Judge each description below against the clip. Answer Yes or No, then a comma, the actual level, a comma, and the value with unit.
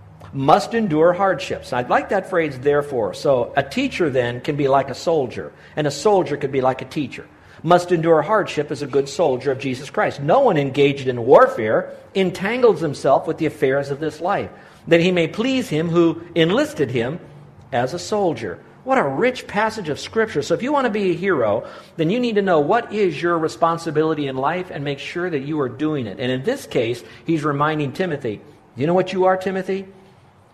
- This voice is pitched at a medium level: Yes, medium, 160 Hz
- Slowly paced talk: No, fast, 205 wpm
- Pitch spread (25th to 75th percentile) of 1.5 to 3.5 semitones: No, average, 5.0 semitones